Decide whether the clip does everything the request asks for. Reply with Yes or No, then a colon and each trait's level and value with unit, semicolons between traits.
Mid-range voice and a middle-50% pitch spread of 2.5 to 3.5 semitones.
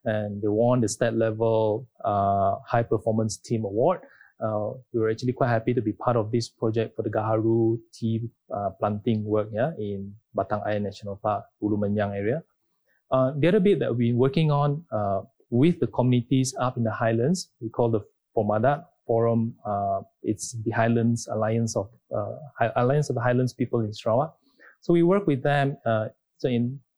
No: low, 115 Hz; average, 2.8 semitones